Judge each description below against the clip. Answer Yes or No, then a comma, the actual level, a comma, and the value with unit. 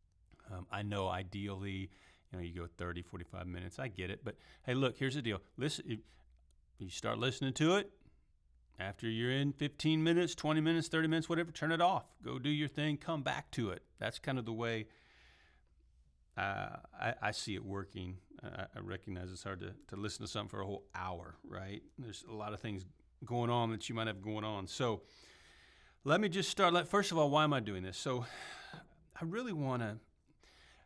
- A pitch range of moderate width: No, wide, 7.6 semitones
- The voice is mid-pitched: No, low, 105 Hz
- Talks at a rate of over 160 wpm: Yes, fast, 205 wpm